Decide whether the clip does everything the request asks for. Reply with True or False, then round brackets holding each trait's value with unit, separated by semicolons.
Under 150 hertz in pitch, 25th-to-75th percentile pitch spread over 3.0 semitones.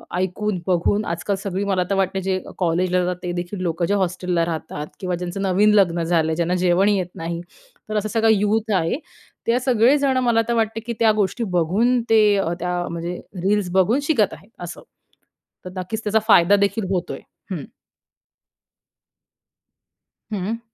False (190 Hz; 3.4 semitones)